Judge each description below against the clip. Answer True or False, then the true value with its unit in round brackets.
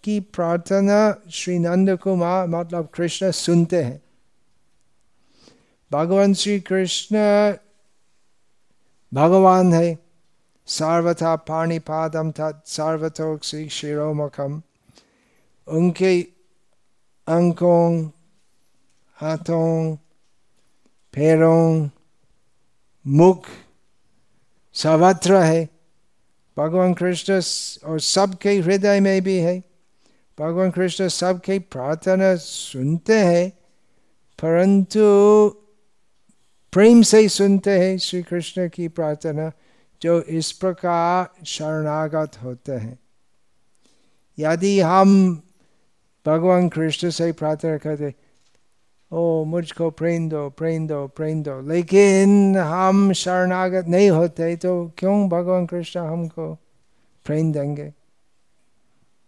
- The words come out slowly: True (85 wpm)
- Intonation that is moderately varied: True (3.0 semitones)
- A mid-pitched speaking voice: True (170 Hz)